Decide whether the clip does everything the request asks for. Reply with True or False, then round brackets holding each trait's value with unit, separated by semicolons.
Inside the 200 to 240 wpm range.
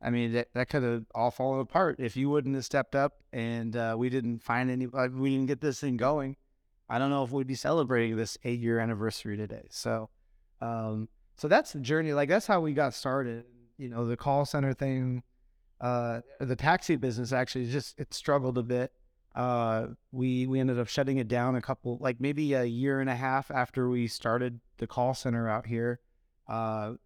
True (205 wpm)